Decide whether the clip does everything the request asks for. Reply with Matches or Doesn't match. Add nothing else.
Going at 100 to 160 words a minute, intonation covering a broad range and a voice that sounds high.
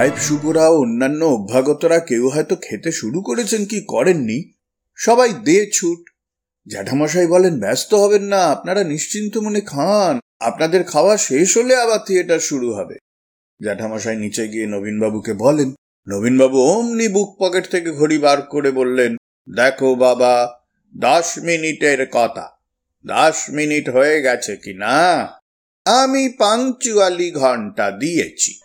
Doesn't match